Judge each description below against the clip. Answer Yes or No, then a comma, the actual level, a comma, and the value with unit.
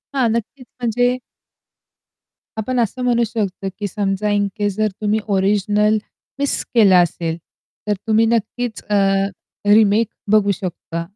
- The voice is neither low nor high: No, high, 210 Hz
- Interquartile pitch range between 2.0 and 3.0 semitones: Yes, narrow, 2.5 semitones